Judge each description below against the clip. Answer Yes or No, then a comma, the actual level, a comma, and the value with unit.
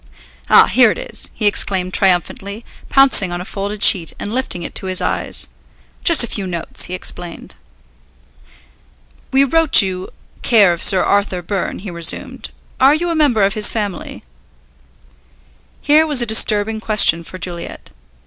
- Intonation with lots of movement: No, average, 4.5 semitones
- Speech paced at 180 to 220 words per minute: No, average, 160 wpm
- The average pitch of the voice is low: No, high, 200 Hz